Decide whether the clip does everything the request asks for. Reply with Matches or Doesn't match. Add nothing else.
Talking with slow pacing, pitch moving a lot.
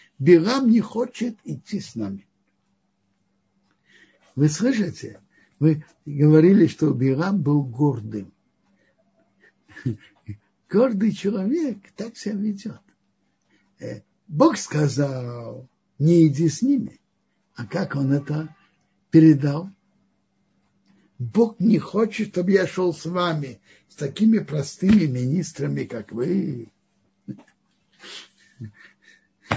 Matches